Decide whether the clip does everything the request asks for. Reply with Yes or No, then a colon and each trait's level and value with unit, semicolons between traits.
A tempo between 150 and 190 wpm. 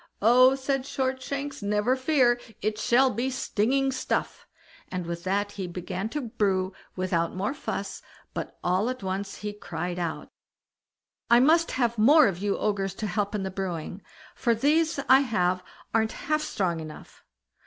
Yes: average, 165 wpm